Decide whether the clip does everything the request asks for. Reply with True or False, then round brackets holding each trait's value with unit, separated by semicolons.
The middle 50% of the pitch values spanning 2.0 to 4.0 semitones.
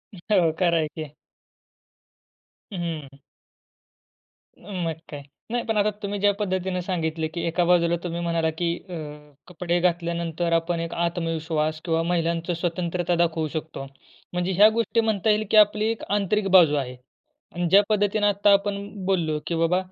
True (3.2 semitones)